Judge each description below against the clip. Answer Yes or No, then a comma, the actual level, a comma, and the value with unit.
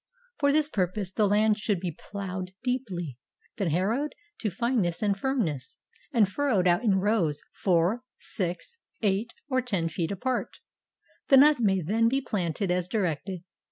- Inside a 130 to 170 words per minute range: Yes, average, 155 wpm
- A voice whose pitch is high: Yes, high, 200 Hz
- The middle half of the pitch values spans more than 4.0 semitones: Yes, average, 4.8 semitones